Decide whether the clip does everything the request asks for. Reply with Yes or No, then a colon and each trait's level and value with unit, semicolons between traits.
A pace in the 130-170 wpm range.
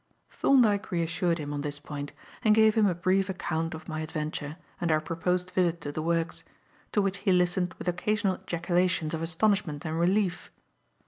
No: average, 180 wpm